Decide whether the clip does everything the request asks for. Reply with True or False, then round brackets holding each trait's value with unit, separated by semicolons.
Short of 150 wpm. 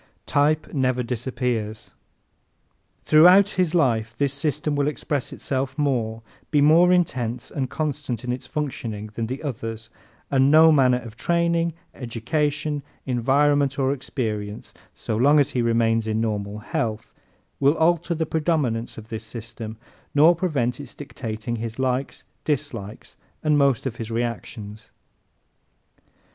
True (135 wpm)